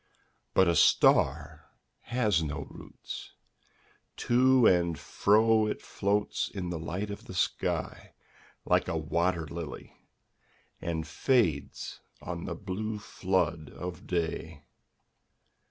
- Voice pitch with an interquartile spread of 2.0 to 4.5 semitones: Yes, average, 4.2 semitones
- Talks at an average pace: No, slow, 110 wpm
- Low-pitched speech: Yes, very low, 90 Hz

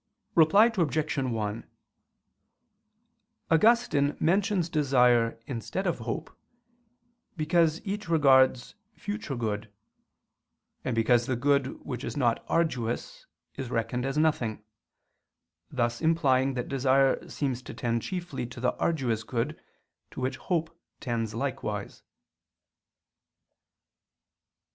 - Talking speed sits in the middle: No, slow, 105 wpm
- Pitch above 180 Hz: No, low, 135 Hz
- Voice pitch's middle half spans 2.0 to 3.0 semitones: No, average, 5.1 semitones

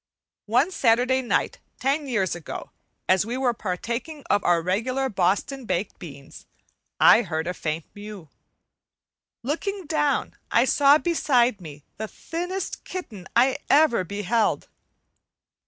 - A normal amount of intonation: No, wide, 6.8 semitones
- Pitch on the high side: Yes, high, 235 Hz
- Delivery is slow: Yes, slow, 125 wpm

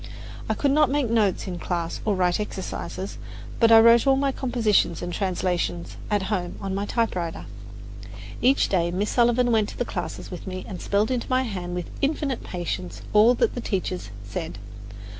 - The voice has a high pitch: Yes, high, 205 Hz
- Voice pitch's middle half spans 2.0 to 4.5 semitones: No, average, 5.1 semitones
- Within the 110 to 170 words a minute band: No, average, 180 wpm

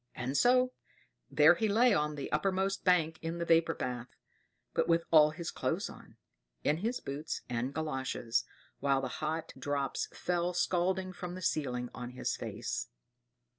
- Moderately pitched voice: Yes, medium, 160 Hz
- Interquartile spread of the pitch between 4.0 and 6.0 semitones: Yes, average, 4.6 semitones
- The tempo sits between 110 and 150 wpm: No, average, 160 wpm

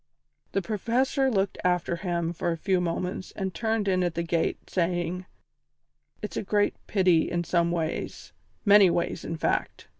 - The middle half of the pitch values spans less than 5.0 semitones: Yes, average, 2.8 semitones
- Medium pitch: Yes, medium, 180 Hz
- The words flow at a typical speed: Yes, average, 160 wpm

